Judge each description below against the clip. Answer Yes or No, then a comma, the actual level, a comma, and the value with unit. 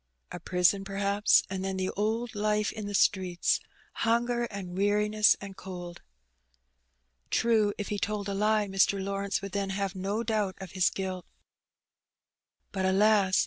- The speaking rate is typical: Yes, average, 155 wpm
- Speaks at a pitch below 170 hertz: No, high, 200 Hz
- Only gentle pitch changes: Yes, narrow, 1.8 semitones